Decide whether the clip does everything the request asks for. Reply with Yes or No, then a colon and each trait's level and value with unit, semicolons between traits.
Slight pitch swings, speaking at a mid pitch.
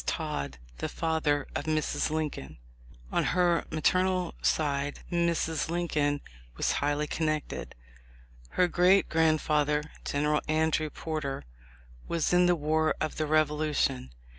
Yes: narrow, 1.9 semitones; medium, 155 Hz